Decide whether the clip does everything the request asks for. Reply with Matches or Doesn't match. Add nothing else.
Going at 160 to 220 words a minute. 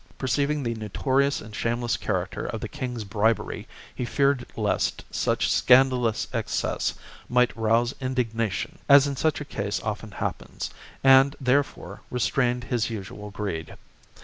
Doesn't match